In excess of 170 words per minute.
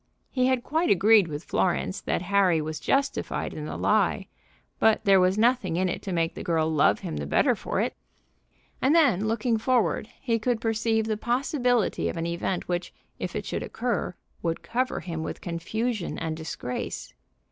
Yes: average, 180 wpm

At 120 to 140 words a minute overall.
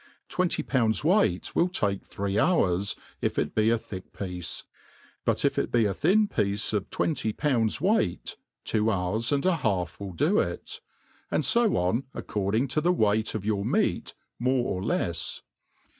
No: average, 170 wpm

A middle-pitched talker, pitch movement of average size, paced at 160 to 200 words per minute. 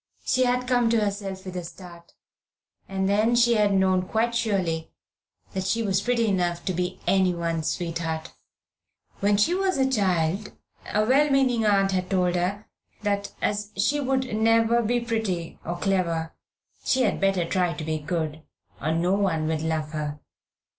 No: high, 195 Hz; average, 4.8 semitones; average, 165 wpm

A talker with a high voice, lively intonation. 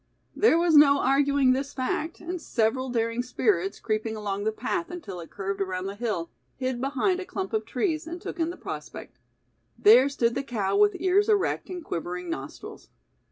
Yes: very high, 255 Hz; wide, 8.1 semitones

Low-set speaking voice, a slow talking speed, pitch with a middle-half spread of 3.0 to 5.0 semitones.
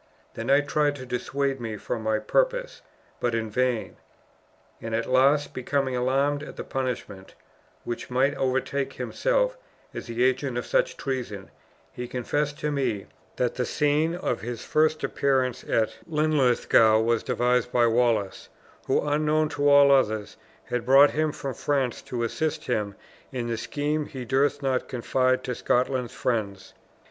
No: low, 130 Hz; average, 155 wpm; average, 3.4 semitones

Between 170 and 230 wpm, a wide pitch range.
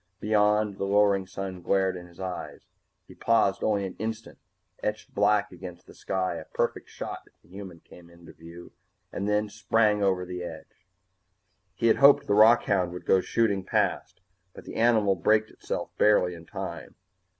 No: average, 180 wpm; average, 2.8 semitones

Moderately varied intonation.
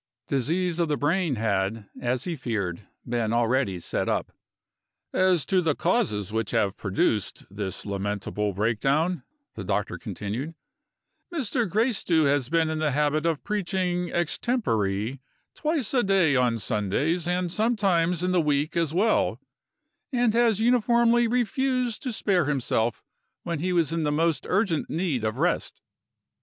No: wide, 8.3 semitones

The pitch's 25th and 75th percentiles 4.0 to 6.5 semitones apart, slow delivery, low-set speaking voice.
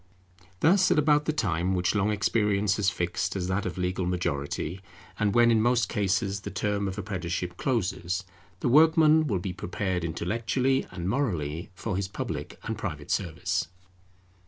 No: average, 4.5 semitones; average, 160 wpm; low, 100 Hz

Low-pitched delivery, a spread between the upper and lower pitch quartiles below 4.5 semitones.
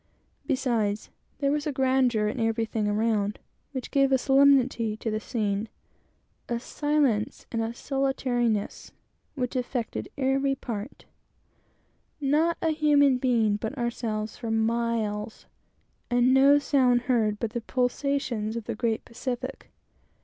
No: high, 245 Hz; average, 3.5 semitones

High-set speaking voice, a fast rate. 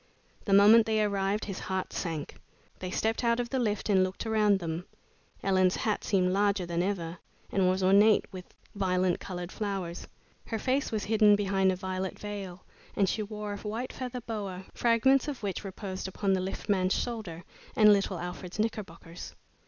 No: high, 195 Hz; average, 175 wpm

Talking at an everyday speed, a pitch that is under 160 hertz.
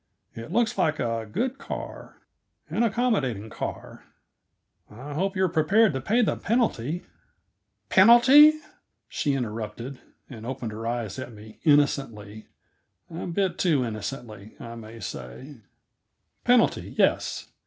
No: slow, 130 wpm; low, 135 Hz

